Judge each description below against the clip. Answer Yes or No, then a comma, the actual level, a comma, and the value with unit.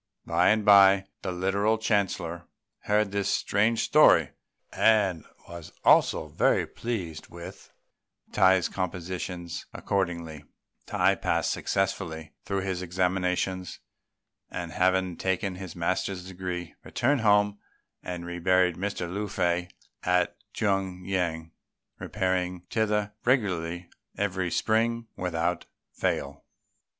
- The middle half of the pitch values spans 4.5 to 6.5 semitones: No, narrow, 2.4 semitones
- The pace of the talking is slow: Yes, slow, 105 wpm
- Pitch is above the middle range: No, very low, 95 Hz